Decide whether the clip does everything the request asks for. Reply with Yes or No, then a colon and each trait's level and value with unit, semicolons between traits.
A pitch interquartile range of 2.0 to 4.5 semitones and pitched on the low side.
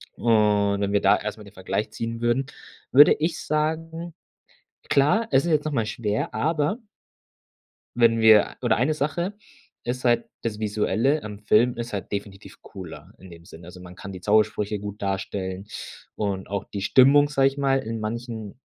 No: average, 5.1 semitones; low, 110 Hz